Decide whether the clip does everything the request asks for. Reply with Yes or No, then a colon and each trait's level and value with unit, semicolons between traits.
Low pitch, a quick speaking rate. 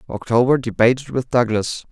No: low, 120 Hz; slow, 125 wpm